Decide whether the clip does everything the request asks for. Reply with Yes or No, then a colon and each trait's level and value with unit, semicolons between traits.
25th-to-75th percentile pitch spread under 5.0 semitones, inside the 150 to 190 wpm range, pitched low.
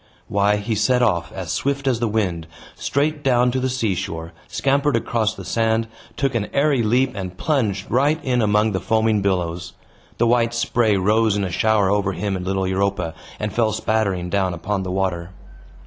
Yes: average, 4.1 semitones; average, 185 wpm; low, 105 Hz